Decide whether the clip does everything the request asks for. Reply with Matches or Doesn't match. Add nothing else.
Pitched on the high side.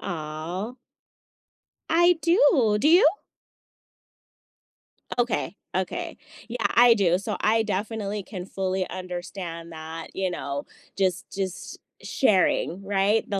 Matches